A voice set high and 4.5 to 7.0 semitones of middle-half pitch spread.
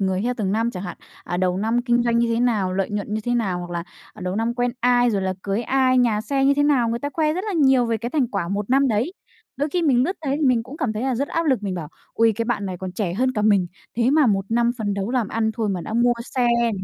No: high, 230 Hz; average, 4.1 semitones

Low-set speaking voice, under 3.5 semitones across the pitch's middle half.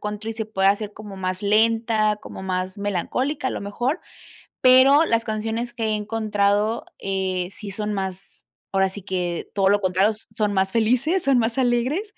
No: high, 210 Hz; average, 3.1 semitones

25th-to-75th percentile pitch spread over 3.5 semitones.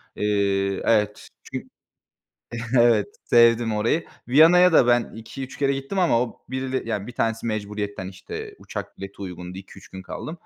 Yes: average, 4.5 semitones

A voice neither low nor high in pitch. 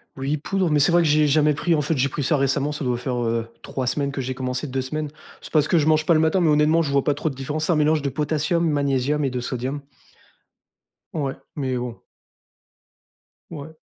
Yes: medium, 145 Hz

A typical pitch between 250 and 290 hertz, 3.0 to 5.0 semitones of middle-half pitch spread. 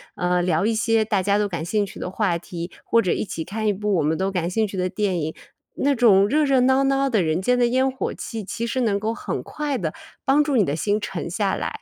No: high, 205 Hz; average, 4.7 semitones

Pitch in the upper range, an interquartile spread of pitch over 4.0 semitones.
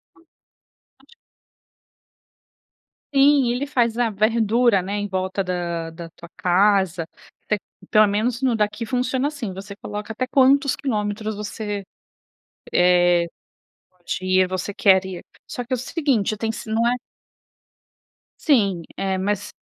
Yes: high, 210 Hz; average, 4.5 semitones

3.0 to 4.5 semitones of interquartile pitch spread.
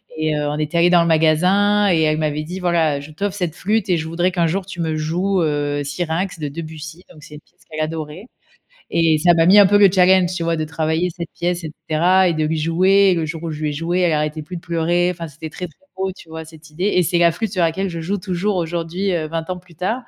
No: narrow, 2.6 semitones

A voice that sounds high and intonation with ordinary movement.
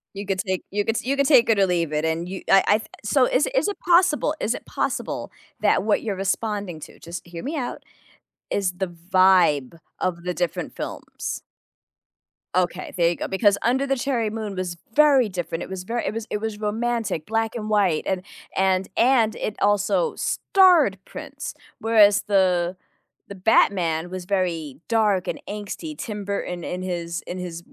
Yes: high, 200 Hz; average, 4.0 semitones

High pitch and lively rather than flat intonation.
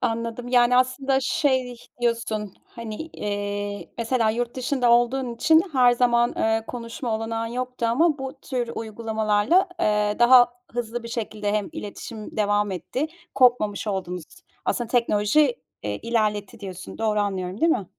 No: high, 230 Hz; average, 3.0 semitones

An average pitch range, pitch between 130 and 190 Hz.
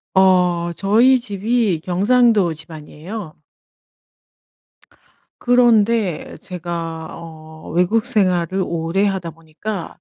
Yes: average, 4.6 semitones; medium, 185 Hz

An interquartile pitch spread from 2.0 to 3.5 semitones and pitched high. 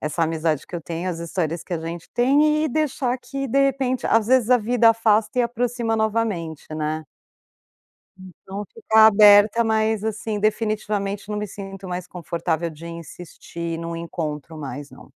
No: average, 5.3 semitones; high, 205 Hz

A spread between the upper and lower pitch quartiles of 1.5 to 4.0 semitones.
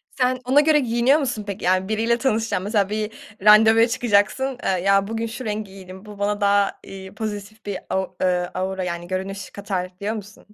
Yes: average, 2.9 semitones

